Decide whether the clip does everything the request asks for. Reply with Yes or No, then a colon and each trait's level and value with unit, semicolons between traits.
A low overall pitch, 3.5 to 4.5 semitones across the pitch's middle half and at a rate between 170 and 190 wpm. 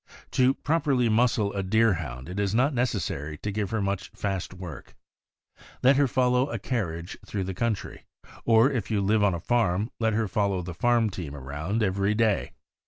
Yes: low, 105 Hz; average, 4.0 semitones; average, 185 wpm